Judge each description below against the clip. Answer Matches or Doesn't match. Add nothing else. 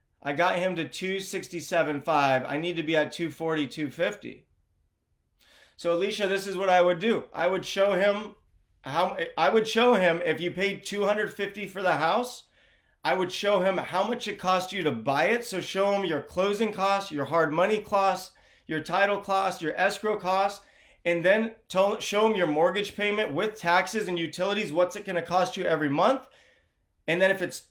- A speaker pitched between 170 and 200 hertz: Matches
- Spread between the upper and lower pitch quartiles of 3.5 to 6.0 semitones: Doesn't match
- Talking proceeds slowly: Doesn't match